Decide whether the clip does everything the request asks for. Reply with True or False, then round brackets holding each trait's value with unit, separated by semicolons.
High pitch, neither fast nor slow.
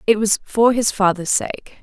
True (210 Hz; 195 wpm)